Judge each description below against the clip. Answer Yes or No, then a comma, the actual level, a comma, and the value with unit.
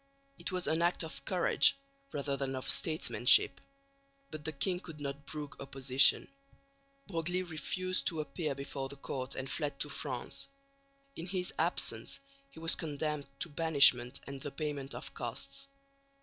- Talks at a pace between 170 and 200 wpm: No, average, 150 wpm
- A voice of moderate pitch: Yes, medium, 150 Hz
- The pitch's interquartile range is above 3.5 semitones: No, average, 3.1 semitones